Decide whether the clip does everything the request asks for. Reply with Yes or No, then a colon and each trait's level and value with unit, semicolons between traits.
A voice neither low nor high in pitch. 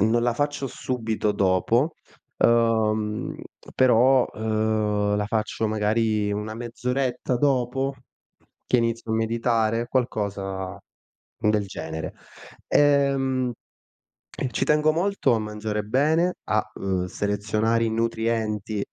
No: low, 115 Hz